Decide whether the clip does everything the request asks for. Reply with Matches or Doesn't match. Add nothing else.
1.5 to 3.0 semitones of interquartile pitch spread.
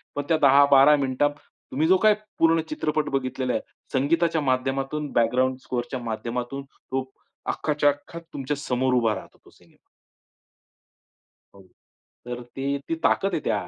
Matches